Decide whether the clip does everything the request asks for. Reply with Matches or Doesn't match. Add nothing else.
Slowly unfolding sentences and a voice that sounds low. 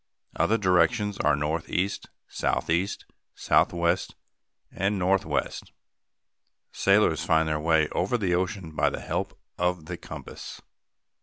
Matches